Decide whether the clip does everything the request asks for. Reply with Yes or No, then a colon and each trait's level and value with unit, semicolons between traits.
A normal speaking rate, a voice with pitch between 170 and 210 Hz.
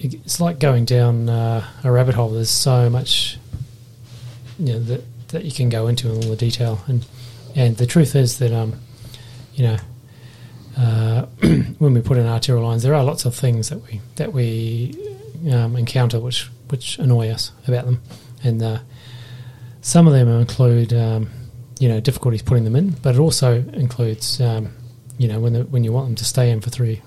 No: average, 195 wpm; low, 120 Hz